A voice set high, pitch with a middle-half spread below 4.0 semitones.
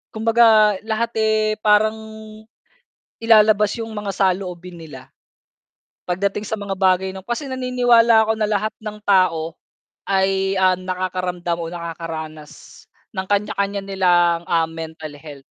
Yes: high, 195 Hz; average, 3.6 semitones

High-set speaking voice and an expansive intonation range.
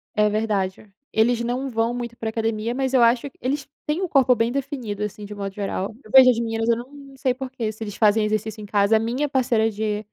No: high, 225 Hz; average, 3.1 semitones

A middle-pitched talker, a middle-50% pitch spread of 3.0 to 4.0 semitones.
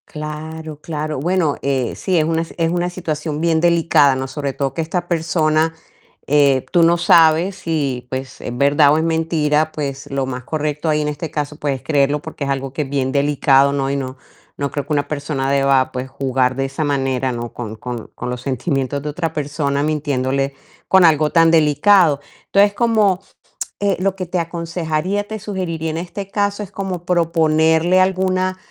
Yes: medium, 155 Hz; average, 3.4 semitones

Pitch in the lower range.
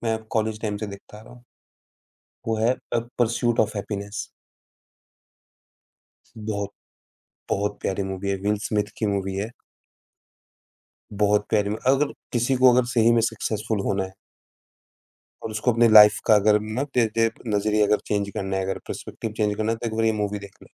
Yes: low, 105 Hz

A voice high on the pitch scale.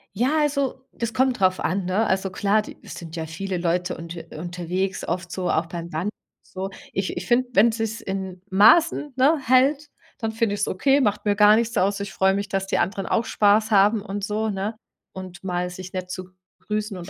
Yes: high, 200 Hz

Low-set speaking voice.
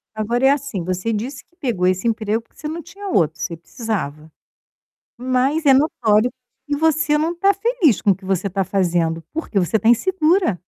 No: high, 230 Hz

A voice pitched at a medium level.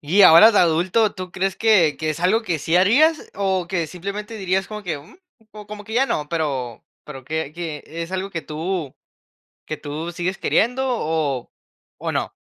Yes: medium, 180 Hz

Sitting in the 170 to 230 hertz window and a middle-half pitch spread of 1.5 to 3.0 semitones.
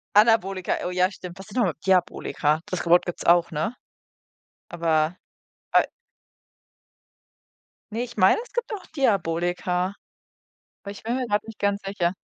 No: medium, 185 Hz; average, 3.6 semitones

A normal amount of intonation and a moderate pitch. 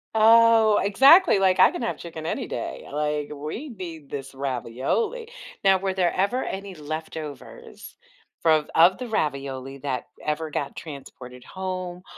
No: wide, 5.7 semitones; medium, 165 Hz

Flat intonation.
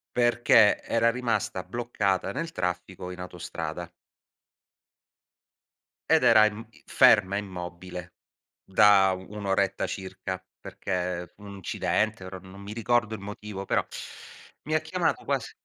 No: average, 3.1 semitones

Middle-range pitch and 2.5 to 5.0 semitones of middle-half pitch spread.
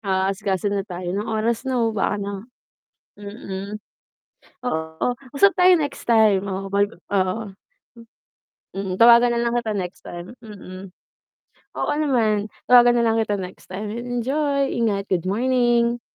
No: high, 215 Hz; average, 3.7 semitones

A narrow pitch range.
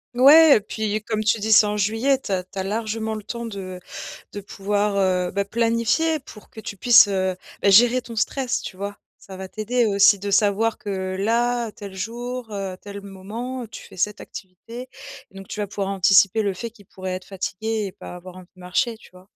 No: average, 3.0 semitones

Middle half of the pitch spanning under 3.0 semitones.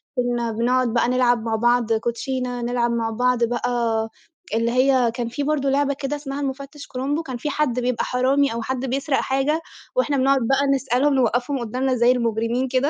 Yes: narrow, 2.4 semitones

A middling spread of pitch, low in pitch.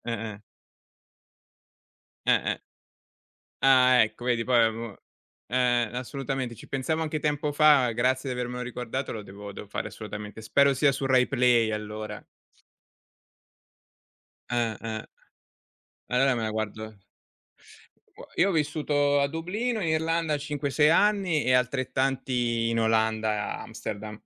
Yes: average, 4.2 semitones; low, 125 Hz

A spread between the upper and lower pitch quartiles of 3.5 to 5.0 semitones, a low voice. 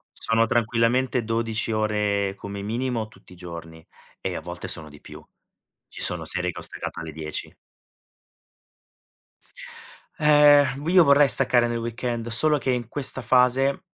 Yes: average, 4.5 semitones; low, 115 Hz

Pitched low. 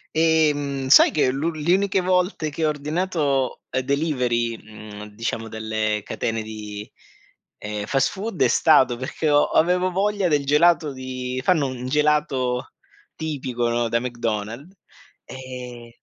Yes: low, 130 Hz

